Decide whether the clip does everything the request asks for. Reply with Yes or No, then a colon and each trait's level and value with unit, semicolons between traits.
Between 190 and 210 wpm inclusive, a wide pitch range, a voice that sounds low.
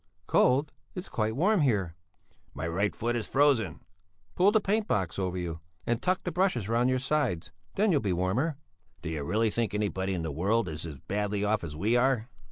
Yes: average, 195 wpm; wide, 6.9 semitones; low, 110 Hz